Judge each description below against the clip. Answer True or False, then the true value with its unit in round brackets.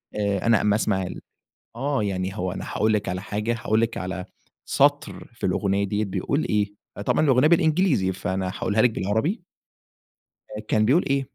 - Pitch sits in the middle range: False (105 Hz)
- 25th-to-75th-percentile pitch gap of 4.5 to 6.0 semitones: True (4.8 semitones)